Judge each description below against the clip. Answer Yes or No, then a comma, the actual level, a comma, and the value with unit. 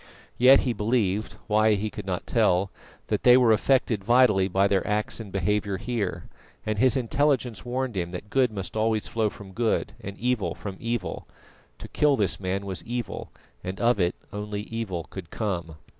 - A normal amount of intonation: Yes, average, 3.7 semitones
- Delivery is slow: No, average, 180 wpm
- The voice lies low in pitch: Yes, low, 105 Hz